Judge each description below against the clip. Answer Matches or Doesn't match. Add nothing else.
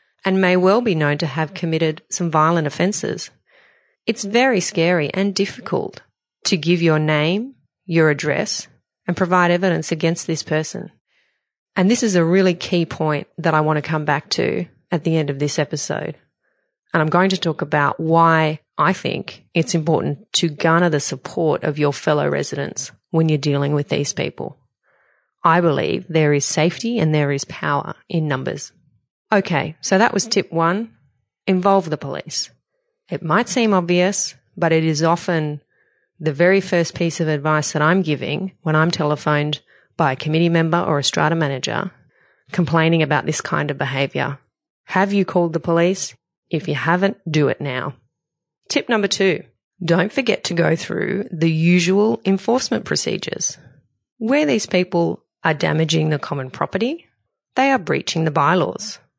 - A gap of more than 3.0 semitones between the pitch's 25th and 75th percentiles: Matches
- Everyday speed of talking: Matches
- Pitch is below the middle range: Doesn't match